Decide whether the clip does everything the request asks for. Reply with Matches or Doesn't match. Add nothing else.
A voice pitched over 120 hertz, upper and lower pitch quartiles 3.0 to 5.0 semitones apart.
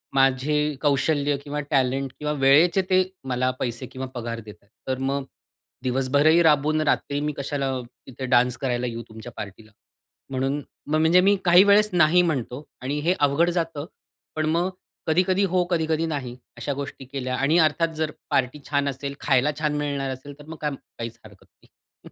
Matches